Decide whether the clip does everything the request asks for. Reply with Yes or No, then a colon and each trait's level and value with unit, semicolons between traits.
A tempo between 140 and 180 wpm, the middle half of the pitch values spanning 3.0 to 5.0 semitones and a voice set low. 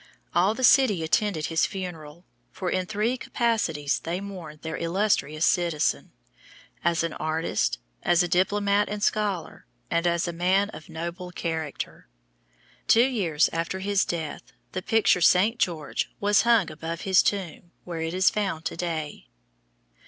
No: average, 150 wpm; average, 3.8 semitones; medium, 175 Hz